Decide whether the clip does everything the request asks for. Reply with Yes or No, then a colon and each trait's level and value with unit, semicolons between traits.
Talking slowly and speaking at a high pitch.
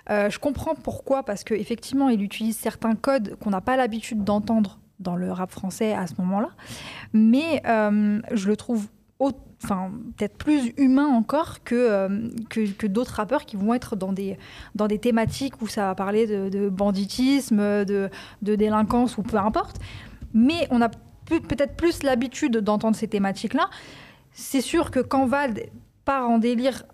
No: average, 175 wpm; high, 225 Hz